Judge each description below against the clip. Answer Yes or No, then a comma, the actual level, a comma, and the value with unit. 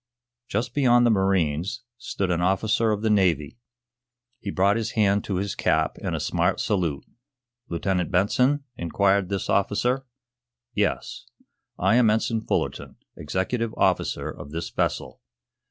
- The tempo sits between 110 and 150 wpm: Yes, average, 140 wpm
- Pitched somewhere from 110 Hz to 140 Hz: No, low, 100 Hz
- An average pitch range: Yes, average, 3.7 semitones